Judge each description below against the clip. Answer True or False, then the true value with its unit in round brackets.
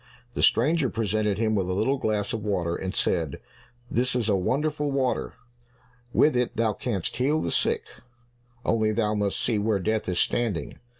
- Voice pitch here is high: False (110 Hz)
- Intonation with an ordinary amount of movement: True (3.6 semitones)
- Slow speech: False (175 wpm)